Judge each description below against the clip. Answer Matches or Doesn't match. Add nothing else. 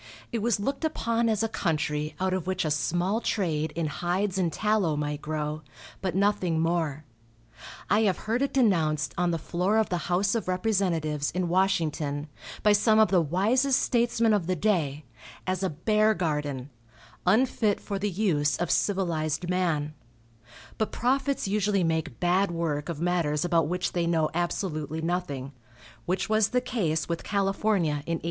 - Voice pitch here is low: Doesn't match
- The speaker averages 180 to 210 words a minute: Doesn't match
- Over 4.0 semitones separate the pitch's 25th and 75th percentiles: Matches